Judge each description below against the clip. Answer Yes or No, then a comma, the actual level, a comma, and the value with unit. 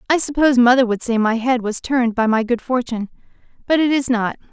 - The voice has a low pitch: No, high, 245 Hz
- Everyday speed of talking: No, fast, 225 wpm